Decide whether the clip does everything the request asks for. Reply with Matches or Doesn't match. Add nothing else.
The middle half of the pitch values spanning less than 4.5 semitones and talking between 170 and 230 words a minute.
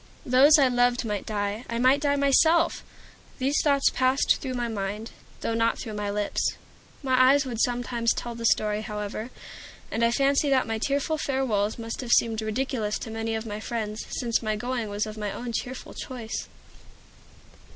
Matches